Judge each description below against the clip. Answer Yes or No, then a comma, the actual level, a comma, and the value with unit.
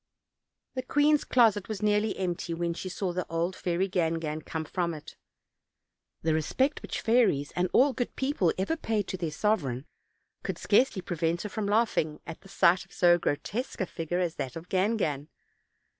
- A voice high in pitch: No, medium, 180 Hz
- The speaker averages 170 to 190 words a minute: Yes, average, 175 wpm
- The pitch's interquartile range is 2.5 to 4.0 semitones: No, average, 4.5 semitones